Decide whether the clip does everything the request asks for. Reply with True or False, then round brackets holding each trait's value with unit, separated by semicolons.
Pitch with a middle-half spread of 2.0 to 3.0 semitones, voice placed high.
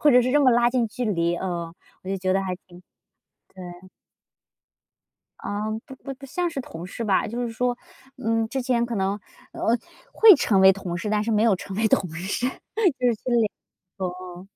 False (4.5 semitones; 215 Hz)